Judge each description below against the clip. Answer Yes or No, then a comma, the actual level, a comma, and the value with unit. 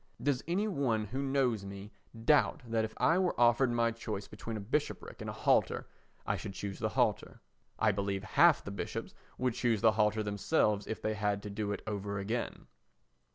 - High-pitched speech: No, low, 110 Hz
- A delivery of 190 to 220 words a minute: Yes, average, 195 wpm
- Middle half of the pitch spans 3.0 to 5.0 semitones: Yes, average, 3.7 semitones